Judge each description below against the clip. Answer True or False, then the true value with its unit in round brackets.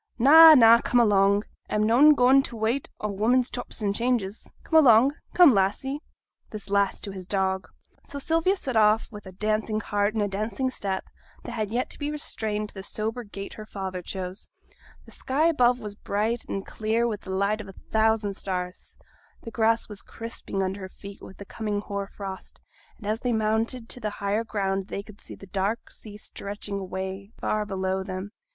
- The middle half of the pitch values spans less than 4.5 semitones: True (2.9 semitones)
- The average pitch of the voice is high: True (210 Hz)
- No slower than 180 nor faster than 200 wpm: True (195 wpm)